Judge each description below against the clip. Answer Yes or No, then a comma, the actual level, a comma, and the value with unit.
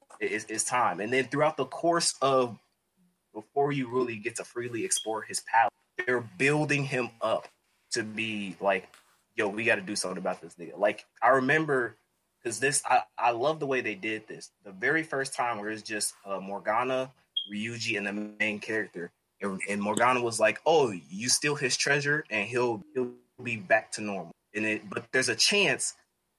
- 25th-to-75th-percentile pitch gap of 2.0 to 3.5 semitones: No, average, 4.7 semitones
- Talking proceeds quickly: No, average, 190 wpm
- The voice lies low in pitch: Yes, low, 120 Hz